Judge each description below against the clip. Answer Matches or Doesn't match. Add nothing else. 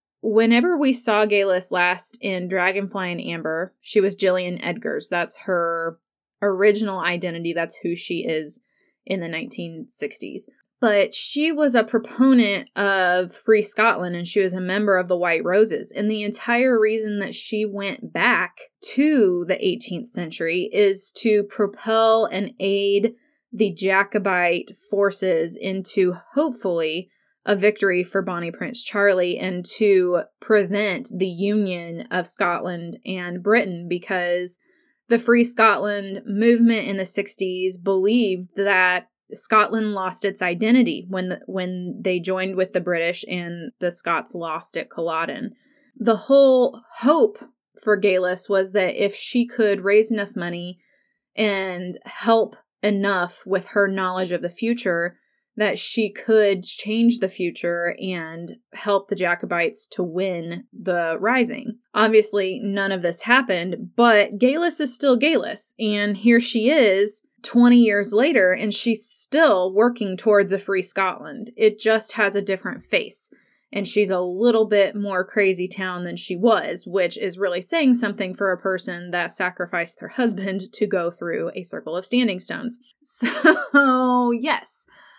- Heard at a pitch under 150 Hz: Doesn't match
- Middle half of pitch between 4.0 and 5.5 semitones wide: Doesn't match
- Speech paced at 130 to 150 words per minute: Matches